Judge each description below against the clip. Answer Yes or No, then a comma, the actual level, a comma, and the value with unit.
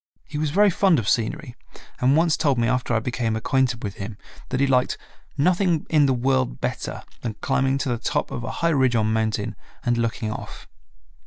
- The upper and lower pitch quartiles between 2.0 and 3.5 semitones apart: No, average, 3.9 semitones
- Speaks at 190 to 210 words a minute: Yes, average, 200 wpm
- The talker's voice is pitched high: No, low, 125 Hz